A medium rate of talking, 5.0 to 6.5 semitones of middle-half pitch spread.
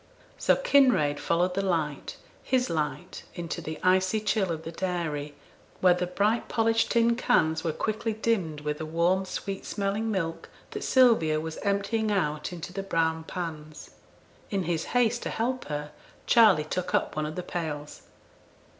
Yes: average, 165 wpm; wide, 5.4 semitones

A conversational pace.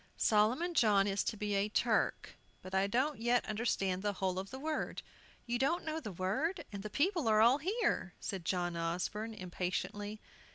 Yes: average, 180 wpm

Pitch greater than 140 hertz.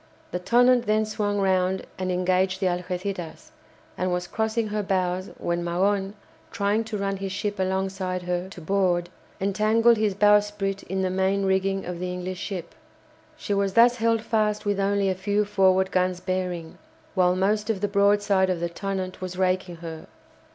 Yes: high, 190 Hz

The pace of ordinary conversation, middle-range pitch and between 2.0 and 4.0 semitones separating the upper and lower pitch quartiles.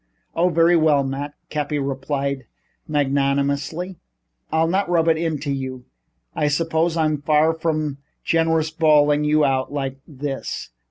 No: slow, 130 wpm; medium, 150 Hz; narrow, 2.6 semitones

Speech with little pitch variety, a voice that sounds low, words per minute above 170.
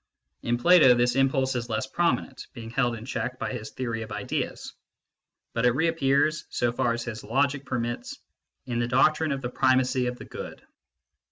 Yes: narrow, 2.3 semitones; low, 125 Hz; average, 180 wpm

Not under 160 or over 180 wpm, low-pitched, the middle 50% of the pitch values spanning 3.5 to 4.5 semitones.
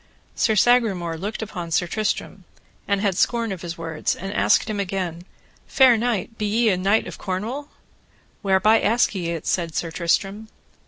No: average, 170 wpm; high, 195 Hz; average, 3.9 semitones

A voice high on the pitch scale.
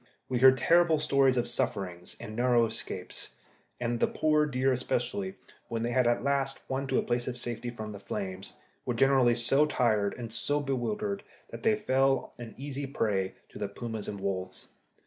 No: low, 125 Hz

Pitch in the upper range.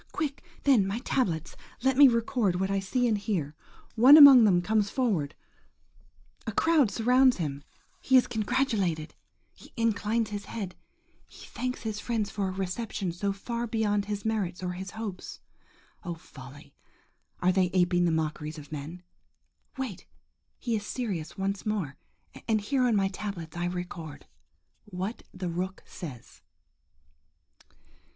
Yes: high, 200 Hz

